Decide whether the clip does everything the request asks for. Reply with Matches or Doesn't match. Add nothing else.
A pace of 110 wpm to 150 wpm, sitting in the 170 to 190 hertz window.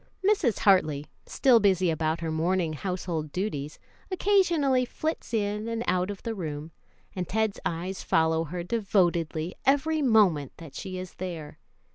Matches